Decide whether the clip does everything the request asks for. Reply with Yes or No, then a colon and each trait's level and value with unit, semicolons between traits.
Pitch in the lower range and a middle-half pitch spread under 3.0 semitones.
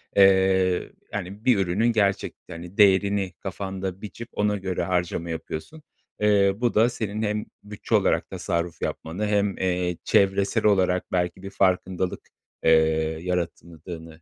Yes: very low, 95 Hz; narrow, 2.5 semitones